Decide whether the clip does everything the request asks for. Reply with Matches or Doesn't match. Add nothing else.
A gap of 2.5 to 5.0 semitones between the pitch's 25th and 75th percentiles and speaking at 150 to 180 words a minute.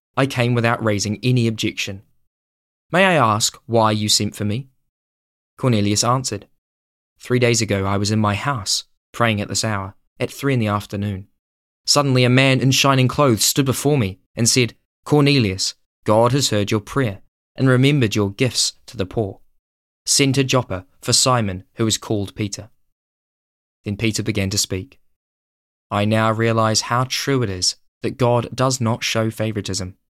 Matches